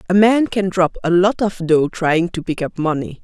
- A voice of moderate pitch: Yes, medium, 180 Hz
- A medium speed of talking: No, fast, 240 wpm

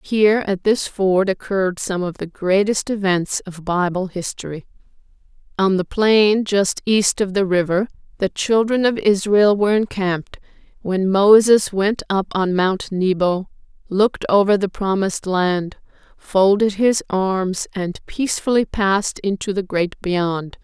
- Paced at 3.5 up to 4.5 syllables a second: Yes, 4.2 syllables/s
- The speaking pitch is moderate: No, high, 195 Hz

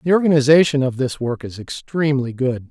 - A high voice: No, low, 135 Hz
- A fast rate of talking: No, average, 180 wpm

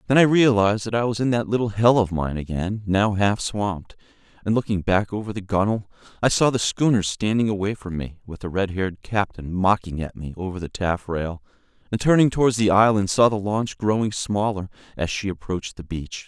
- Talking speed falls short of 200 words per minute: No, fast, 205 wpm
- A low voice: Yes, low, 100 Hz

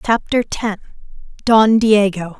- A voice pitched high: Yes, high, 210 Hz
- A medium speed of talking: No, slow, 100 wpm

